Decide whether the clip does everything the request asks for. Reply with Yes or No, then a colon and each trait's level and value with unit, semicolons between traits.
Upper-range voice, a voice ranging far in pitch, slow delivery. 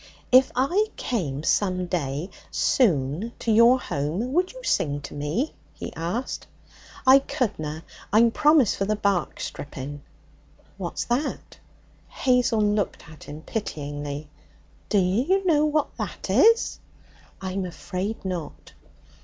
Yes: high, 200 Hz; wide, 8.3 semitones; slow, 125 wpm